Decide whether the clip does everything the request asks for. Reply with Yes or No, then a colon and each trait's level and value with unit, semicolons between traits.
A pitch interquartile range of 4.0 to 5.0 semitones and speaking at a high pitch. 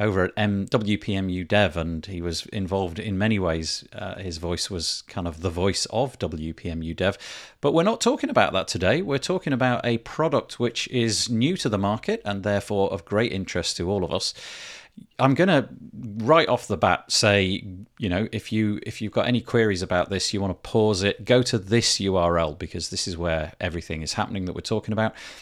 No: average, 4.4 semitones; low, 105 Hz